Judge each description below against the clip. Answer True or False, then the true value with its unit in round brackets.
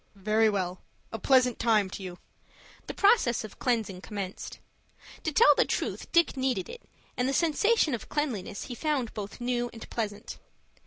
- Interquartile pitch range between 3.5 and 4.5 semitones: False (5.2 semitones)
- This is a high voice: True (240 Hz)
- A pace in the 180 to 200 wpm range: False (165 wpm)